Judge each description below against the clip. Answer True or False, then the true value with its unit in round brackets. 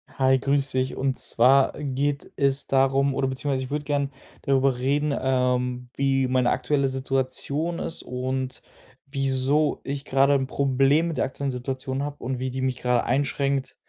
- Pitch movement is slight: True (1.3 semitones)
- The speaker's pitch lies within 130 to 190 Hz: True (135 Hz)